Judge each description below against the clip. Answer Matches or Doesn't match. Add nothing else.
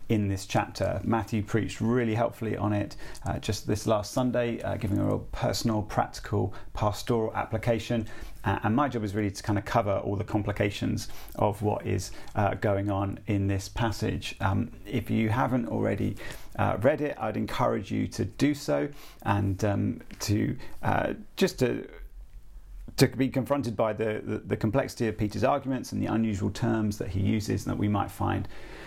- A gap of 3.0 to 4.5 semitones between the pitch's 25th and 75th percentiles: Doesn't match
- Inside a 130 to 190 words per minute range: Matches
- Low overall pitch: Matches